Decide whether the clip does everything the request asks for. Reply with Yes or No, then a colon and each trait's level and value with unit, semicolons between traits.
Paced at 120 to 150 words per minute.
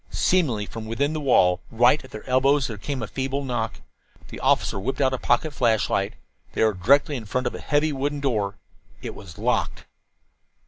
No: average, 190 wpm